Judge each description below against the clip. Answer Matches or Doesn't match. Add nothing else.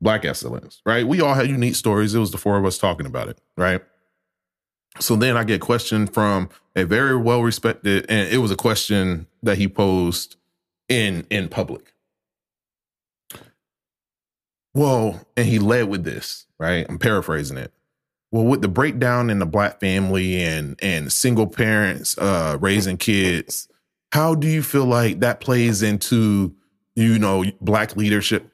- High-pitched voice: Doesn't match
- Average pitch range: Matches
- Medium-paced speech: Matches